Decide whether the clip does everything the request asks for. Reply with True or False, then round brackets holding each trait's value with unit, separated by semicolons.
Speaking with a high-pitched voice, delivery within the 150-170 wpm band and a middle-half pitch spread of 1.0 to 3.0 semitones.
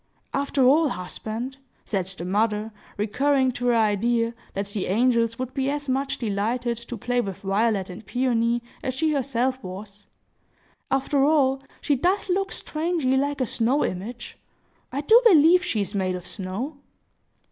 False (245 Hz; 155 wpm; 4.8 semitones)